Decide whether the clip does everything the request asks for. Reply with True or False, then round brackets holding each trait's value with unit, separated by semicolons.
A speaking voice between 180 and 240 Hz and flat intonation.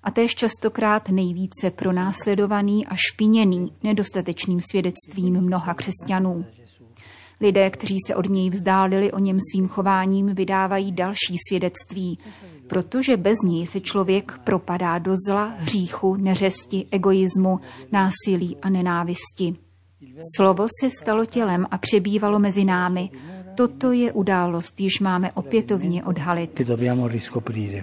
True (190 Hz; 2.1 semitones)